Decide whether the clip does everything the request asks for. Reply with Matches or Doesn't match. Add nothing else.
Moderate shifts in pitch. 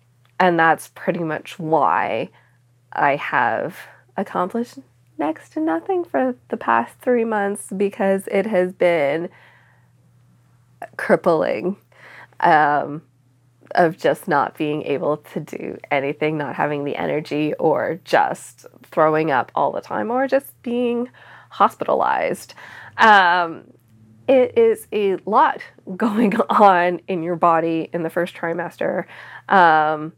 Doesn't match